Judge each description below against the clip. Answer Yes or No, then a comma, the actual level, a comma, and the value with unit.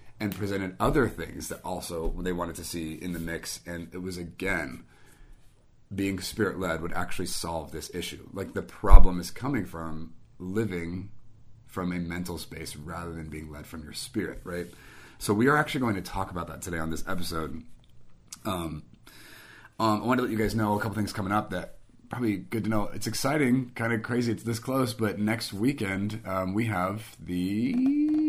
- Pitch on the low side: Yes, very low, 95 Hz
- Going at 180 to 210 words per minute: Yes, average, 195 wpm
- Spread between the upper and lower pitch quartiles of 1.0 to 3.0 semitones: No, average, 4.4 semitones